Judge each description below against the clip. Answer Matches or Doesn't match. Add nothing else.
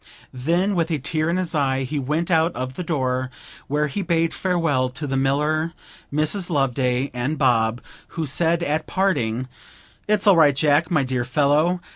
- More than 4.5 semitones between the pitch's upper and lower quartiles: Doesn't match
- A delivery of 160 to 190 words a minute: Matches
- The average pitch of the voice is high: Doesn't match